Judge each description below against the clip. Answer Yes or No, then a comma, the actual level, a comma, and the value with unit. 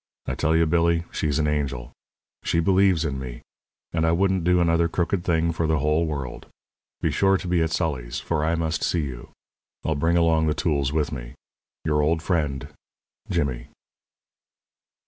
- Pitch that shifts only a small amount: Yes, narrow, 2.3 semitones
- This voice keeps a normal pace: Yes, average, 175 wpm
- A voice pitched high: No, very low, 80 Hz